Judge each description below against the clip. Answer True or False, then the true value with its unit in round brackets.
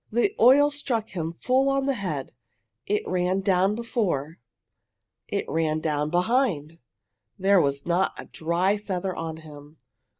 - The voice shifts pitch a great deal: True (6.0 semitones)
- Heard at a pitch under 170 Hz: False (185 Hz)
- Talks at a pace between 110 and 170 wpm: True (140 wpm)